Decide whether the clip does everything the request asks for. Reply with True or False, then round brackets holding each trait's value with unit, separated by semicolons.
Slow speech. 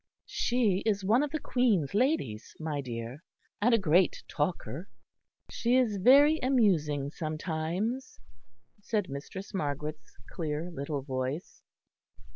True (115 wpm)